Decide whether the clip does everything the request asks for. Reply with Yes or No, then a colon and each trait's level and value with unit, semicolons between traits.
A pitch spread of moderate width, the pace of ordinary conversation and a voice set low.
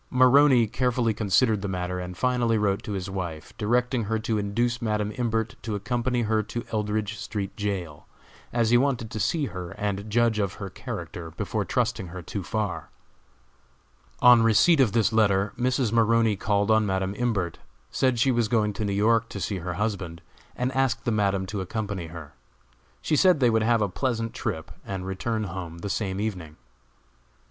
Yes: average, 3.4 semitones; average, 180 wpm; low, 105 Hz